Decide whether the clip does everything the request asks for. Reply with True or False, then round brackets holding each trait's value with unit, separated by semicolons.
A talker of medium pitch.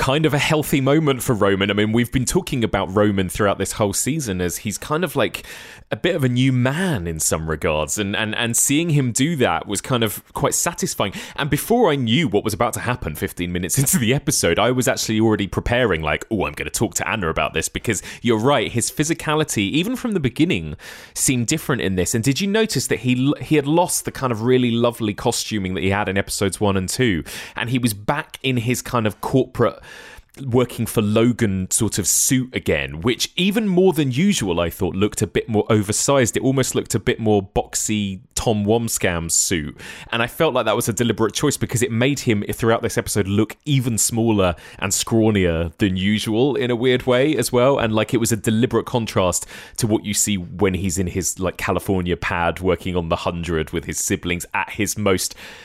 False (115 Hz)